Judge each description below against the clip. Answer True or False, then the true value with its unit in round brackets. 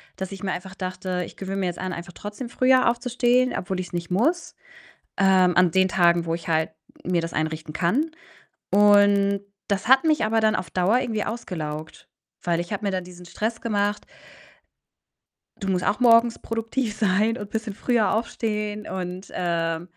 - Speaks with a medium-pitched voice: False (195 Hz)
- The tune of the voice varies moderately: True (3.8 semitones)